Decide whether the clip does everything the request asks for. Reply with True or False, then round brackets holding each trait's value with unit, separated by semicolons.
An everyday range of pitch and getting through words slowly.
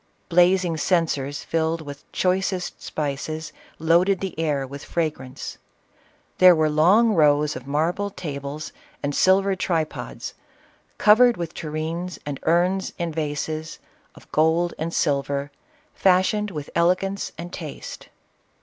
True (3.4 semitones; 120 wpm)